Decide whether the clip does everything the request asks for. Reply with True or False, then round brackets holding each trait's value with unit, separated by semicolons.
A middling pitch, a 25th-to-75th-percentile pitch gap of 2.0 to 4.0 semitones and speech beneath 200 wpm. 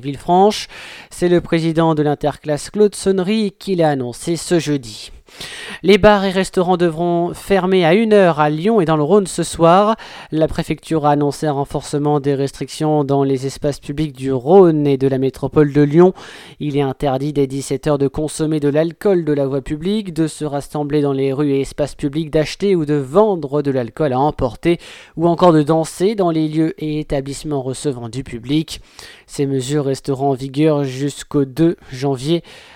True (150 Hz; 3.6 semitones; 180 wpm)